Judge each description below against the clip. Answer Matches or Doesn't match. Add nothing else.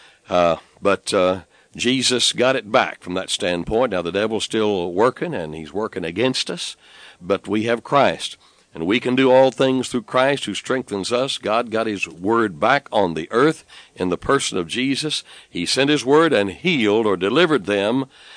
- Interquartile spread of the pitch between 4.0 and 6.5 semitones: Matches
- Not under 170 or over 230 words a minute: Matches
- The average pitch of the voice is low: Matches